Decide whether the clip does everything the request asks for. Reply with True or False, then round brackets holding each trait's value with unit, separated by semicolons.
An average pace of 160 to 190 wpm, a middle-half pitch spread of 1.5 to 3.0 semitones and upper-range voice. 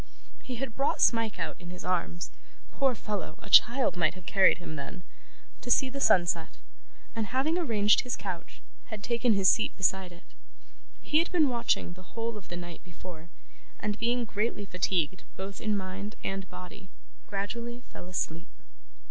False (170 wpm; 4.5 semitones; 200 Hz)